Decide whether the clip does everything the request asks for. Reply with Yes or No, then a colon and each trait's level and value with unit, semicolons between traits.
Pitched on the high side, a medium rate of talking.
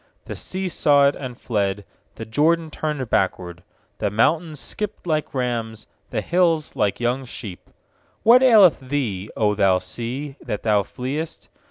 No: low, 130 Hz; average, 150 wpm